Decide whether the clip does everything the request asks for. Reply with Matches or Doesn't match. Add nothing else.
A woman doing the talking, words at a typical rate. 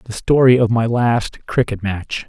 Doesn't match